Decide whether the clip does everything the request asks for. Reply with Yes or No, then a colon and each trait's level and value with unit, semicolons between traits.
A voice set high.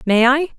Yes: very high, 265 Hz